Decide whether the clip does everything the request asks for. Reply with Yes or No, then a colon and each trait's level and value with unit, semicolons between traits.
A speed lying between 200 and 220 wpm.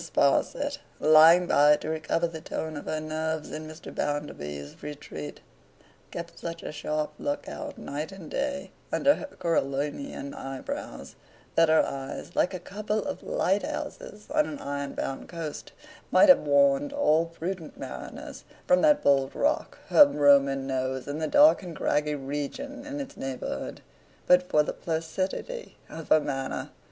No: average, 155 wpm